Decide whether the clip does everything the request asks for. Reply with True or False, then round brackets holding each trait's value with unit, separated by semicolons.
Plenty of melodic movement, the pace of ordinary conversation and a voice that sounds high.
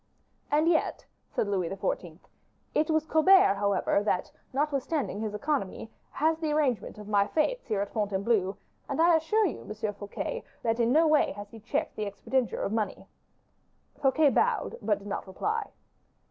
True (7.3 semitones; 165 wpm; 230 Hz)